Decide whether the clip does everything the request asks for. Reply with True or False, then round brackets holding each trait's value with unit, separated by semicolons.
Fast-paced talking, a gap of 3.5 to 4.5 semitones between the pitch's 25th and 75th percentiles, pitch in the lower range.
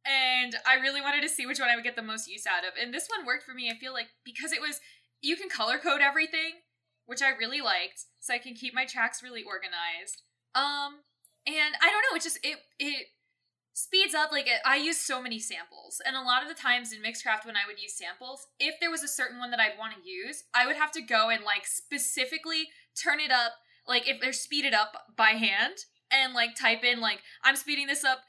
False (240 wpm; 4.1 semitones; 260 Hz)